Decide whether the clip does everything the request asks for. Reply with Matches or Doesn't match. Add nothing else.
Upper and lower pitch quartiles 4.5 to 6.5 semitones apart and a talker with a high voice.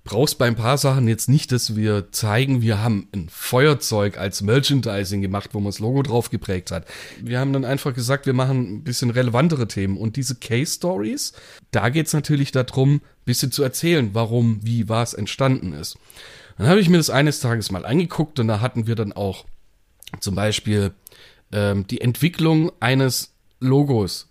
Doesn't match